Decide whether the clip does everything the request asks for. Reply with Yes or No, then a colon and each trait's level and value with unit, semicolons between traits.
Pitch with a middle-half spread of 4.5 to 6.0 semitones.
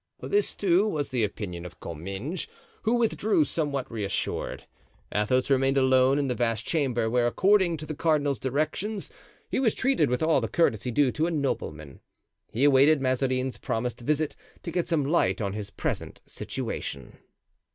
Yes: average, 5.2 semitones